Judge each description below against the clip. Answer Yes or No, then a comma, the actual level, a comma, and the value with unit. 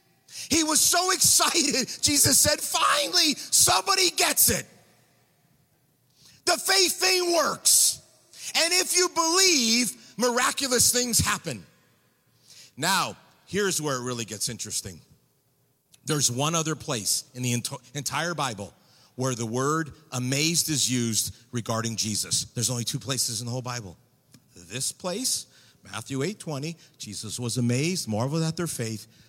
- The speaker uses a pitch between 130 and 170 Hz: Yes, medium, 140 Hz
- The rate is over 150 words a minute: No, slow, 135 wpm